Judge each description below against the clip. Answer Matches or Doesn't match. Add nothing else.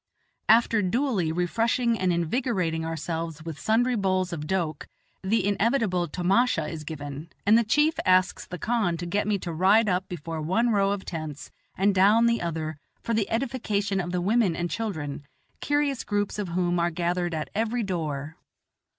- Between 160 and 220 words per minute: Matches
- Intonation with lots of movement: Doesn't match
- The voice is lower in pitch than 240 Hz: Matches